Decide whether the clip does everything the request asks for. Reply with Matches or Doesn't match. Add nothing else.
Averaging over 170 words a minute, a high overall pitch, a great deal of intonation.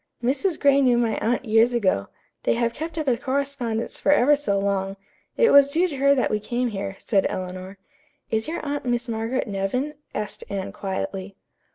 Matches